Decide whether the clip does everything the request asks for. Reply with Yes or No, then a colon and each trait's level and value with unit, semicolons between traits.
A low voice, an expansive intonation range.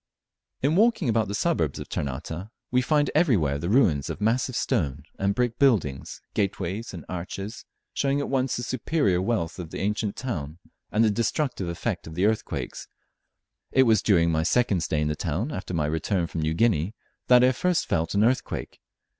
Yes: low, 105 Hz; wide, 6.9 semitones